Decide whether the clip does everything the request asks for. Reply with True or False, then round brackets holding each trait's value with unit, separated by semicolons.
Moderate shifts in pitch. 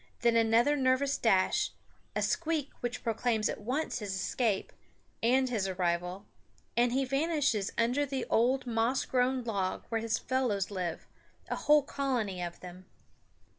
True (4.5 semitones)